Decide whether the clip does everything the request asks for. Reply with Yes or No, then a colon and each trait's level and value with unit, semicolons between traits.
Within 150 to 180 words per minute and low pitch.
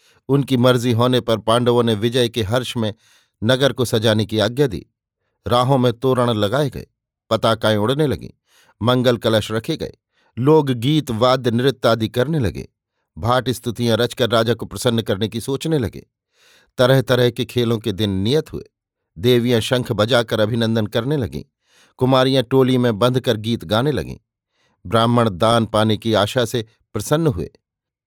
Yes: average, 160 wpm; low, 120 Hz